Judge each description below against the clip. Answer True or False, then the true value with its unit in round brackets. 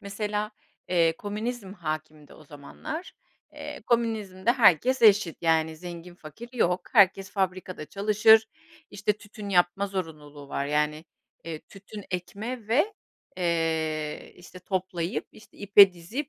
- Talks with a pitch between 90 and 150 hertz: False (190 Hz)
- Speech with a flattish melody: False (4.4 semitones)